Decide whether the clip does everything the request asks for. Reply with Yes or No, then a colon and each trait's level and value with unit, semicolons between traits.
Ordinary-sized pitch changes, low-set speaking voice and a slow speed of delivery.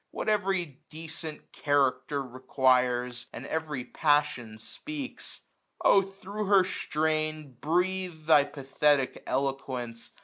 No: average, 5.0 semitones; medium, 150 Hz; slow, 100 wpm